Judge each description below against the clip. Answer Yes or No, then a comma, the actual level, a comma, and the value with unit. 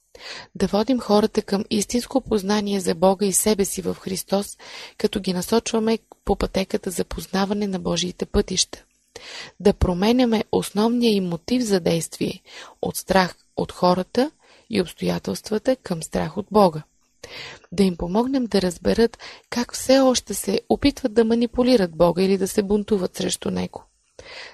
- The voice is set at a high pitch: Yes, high, 210 Hz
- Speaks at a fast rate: No, average, 145 wpm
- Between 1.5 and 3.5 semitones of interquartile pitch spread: No, average, 4.1 semitones